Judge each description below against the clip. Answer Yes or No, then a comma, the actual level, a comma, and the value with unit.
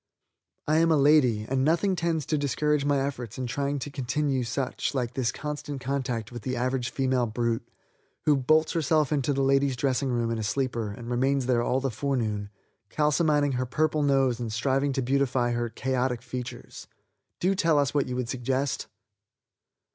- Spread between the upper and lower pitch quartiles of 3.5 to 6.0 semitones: No, average, 2.9 semitones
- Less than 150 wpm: No, average, 180 wpm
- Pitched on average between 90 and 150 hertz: Yes, low, 135 Hz